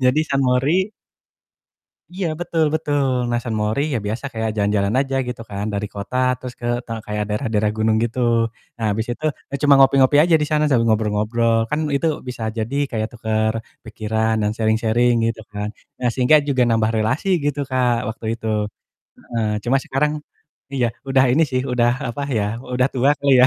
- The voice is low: Yes, low, 120 Hz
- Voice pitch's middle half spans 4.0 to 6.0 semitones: No, average, 3.6 semitones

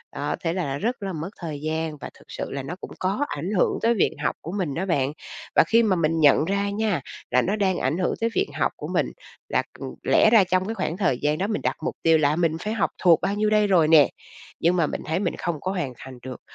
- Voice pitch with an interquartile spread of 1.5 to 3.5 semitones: No, average, 4.6 semitones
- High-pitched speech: No, medium, 175 Hz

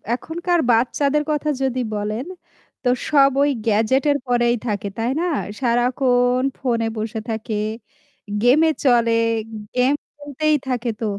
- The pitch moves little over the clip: No, average, 3.7 semitones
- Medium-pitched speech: No, very high, 250 Hz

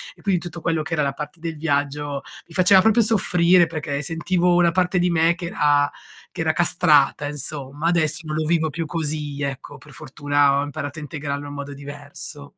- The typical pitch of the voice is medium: Yes, medium, 155 Hz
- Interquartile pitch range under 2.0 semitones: No, average, 2.9 semitones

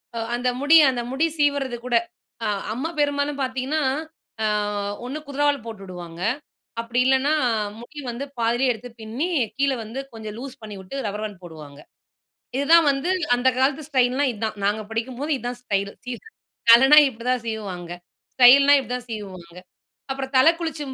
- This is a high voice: Yes, very high, 250 Hz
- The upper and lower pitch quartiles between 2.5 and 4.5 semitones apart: Yes, average, 4.2 semitones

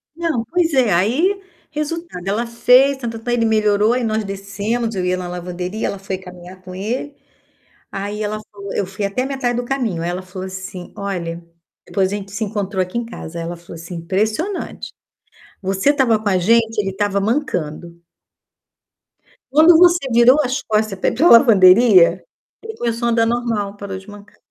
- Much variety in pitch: No, average, 4.2 semitones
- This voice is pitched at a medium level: No, high, 210 Hz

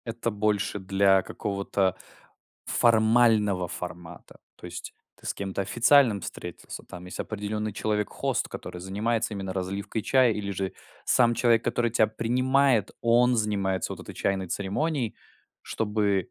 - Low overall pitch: Yes, low, 105 Hz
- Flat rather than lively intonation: No, average, 3.2 semitones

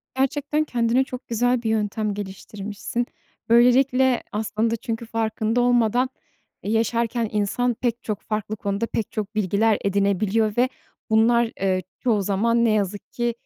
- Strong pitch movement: No, narrow, 2.4 semitones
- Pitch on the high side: Yes, high, 225 Hz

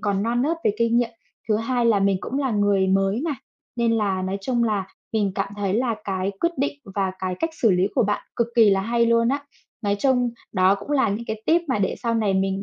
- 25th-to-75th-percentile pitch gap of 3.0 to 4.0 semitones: Yes, average, 3.3 semitones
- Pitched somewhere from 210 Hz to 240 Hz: Yes, high, 215 Hz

